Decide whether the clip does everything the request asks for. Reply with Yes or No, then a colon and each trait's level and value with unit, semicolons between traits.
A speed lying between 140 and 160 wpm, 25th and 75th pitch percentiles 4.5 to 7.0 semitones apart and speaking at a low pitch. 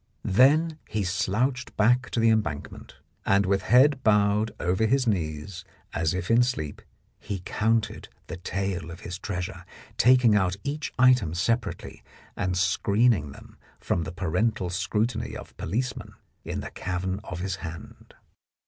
Yes: average, 150 wpm; average, 4.8 semitones; low, 100 Hz